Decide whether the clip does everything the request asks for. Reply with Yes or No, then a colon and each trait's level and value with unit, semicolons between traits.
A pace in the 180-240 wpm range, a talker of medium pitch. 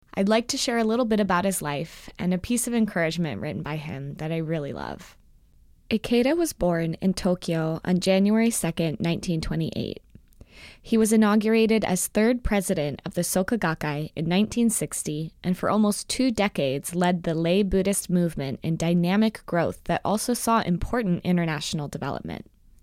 No: average, 165 wpm; medium, 180 Hz